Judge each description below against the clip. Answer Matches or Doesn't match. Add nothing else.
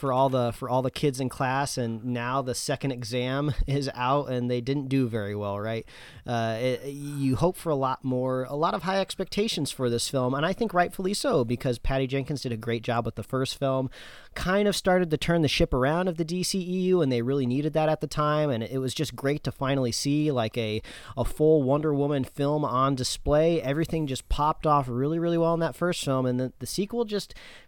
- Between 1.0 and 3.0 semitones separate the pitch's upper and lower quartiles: Doesn't match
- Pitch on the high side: Doesn't match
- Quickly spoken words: Matches